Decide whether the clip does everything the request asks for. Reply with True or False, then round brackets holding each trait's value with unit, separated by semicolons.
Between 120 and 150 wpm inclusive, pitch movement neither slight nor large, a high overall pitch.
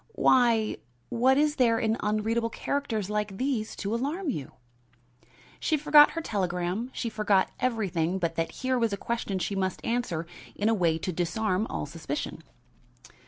False (160 wpm; 4.7 semitones; 215 Hz)